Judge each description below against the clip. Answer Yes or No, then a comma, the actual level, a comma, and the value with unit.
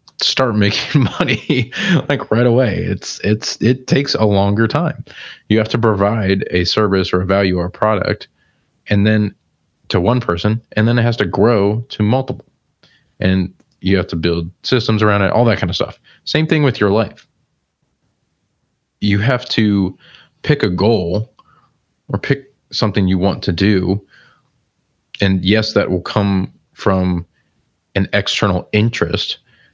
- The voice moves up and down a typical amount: Yes, average, 3.6 semitones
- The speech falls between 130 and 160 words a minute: Yes, average, 155 wpm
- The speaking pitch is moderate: No, low, 105 Hz